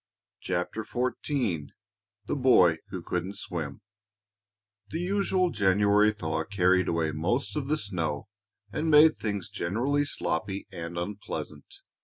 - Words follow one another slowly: Yes, slow, 120 wpm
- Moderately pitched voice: No, low, 100 Hz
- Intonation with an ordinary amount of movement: No, wide, 6.9 semitones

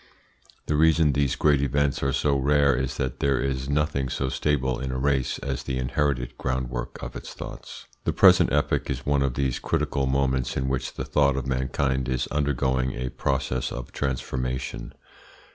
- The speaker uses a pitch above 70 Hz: No, very low, 65 Hz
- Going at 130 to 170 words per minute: No, average, 180 wpm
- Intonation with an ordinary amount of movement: No, narrow, 1.7 semitones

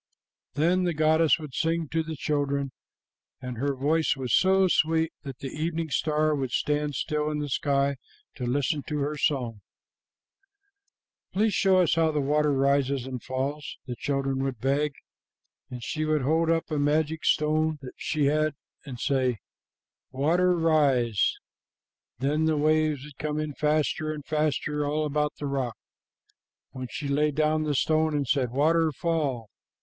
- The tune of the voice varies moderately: No, narrow, 2.3 semitones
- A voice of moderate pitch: Yes, medium, 150 Hz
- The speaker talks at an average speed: Yes, average, 160 wpm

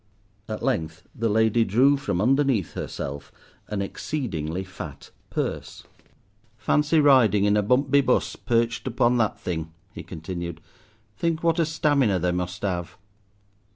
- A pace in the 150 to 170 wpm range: No, average, 140 wpm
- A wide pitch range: Yes, wide, 7.2 semitones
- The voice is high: No, low, 110 Hz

